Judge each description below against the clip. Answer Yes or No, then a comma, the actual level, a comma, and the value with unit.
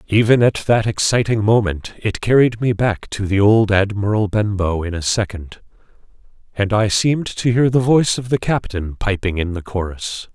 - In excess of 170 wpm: Yes, average, 180 wpm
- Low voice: Yes, low, 105 Hz